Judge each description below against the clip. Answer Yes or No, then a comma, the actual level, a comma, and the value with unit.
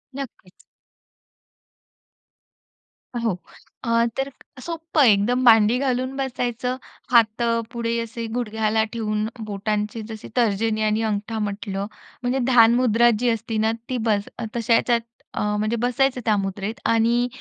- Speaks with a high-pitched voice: Yes, high, 230 Hz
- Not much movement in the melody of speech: Yes, narrow, 2.3 semitones